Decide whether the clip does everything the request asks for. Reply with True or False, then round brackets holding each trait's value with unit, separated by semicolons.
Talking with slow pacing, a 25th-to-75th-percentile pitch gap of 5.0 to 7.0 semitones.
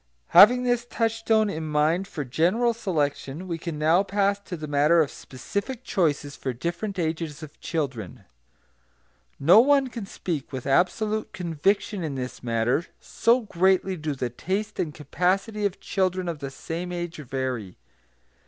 False (155 wpm; 5.5 semitones)